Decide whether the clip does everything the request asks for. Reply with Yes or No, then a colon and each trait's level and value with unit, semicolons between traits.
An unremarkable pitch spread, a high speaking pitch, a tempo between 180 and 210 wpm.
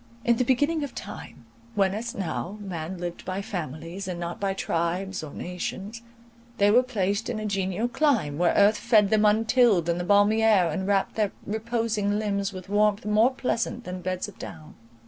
Yes: average, 3.4 semitones; high, 200 Hz; average, 185 wpm